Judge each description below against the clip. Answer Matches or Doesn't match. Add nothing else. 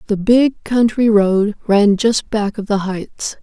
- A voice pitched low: Doesn't match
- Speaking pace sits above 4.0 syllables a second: Doesn't match